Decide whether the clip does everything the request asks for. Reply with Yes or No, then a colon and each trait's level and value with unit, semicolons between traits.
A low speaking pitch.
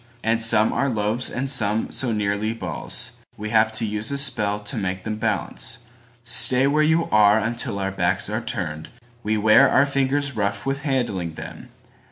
Yes: low, 110 Hz